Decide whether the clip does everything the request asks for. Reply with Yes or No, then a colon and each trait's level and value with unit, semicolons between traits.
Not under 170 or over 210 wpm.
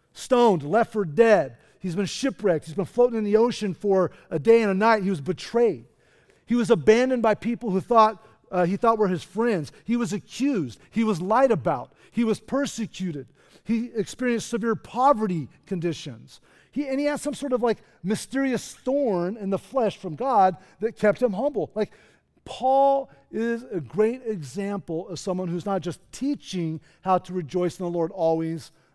Yes: average, 185 wpm